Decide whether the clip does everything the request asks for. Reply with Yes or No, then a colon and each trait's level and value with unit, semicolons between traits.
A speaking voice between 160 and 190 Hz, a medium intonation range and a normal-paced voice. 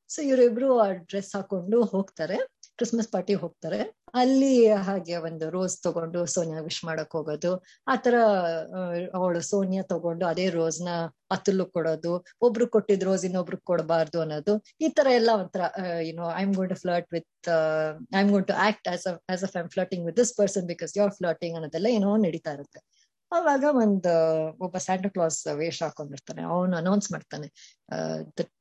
No: medium, 185 Hz; average, 3.5 semitones; fast, 135 wpm